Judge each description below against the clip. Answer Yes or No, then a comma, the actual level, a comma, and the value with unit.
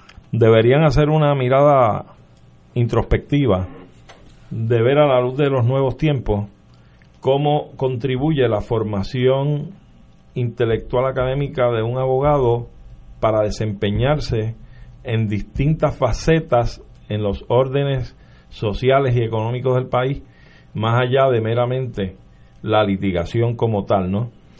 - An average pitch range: Yes, average, 4.0 semitones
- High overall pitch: No, low, 120 Hz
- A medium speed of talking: No, slow, 110 wpm